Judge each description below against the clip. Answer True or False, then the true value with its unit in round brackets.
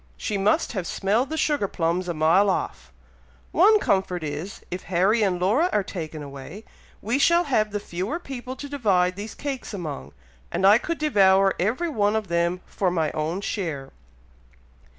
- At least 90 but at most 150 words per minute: False (170 wpm)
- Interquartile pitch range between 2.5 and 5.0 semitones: False (5.4 semitones)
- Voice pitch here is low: False (195 Hz)